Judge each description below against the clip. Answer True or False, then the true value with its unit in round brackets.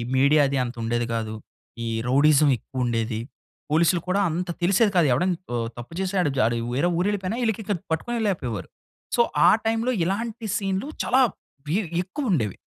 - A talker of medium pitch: True (170 Hz)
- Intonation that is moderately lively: False (8.2 semitones)